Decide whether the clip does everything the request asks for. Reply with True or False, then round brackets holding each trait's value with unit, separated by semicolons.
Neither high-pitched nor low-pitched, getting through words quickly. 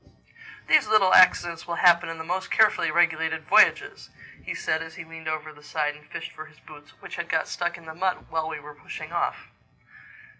True (160 Hz; 210 wpm)